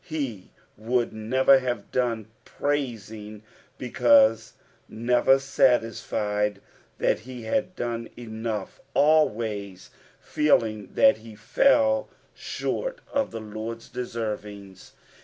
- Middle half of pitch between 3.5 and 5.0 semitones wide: Yes, average, 3.8 semitones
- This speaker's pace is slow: Yes, slow, 95 wpm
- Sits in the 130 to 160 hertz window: No, low, 115 Hz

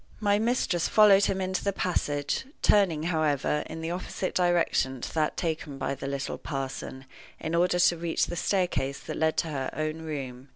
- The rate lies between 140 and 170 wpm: No, average, 180 wpm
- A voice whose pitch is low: No, medium, 160 Hz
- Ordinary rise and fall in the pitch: Yes, average, 4.2 semitones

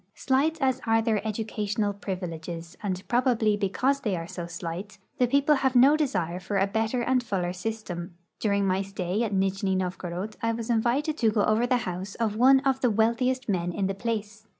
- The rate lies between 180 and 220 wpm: Yes, average, 195 wpm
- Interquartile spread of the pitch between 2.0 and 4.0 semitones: No, average, 4.4 semitones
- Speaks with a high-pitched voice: Yes, high, 215 Hz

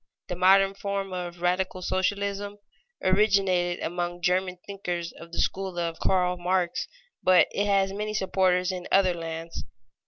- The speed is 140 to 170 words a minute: Yes, average, 145 wpm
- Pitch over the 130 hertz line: Yes, medium, 185 Hz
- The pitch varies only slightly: Yes, narrow, 1.7 semitones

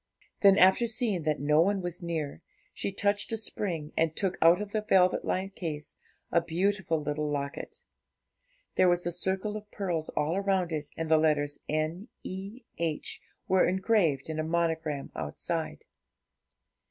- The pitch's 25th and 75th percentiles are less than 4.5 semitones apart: Yes, average, 3.9 semitones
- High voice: No, medium, 175 Hz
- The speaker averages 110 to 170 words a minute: Yes, average, 155 wpm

